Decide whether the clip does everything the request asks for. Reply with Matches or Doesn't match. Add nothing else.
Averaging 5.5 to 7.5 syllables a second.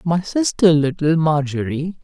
Doesn't match